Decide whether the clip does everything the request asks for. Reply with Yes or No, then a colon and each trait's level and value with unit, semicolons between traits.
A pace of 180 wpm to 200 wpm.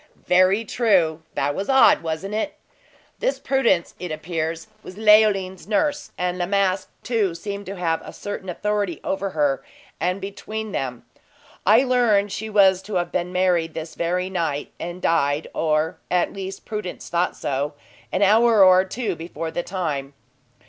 No: average, 160 wpm